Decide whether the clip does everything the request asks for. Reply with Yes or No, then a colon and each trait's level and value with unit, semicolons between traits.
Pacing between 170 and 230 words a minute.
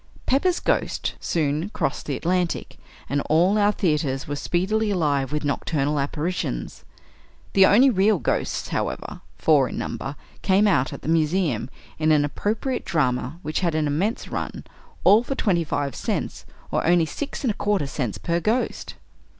No: average, 160 wpm